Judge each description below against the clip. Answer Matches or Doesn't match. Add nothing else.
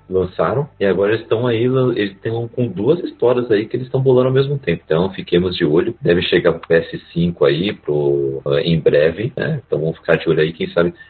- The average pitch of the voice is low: Matches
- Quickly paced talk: Matches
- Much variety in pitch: Matches